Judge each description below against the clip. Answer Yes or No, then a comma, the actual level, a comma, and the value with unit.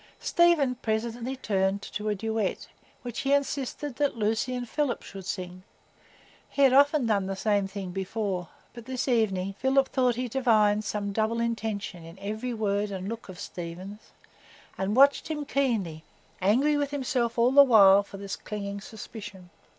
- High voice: Yes, high, 220 Hz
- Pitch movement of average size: Yes, average, 4.4 semitones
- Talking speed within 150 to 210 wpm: Yes, average, 165 wpm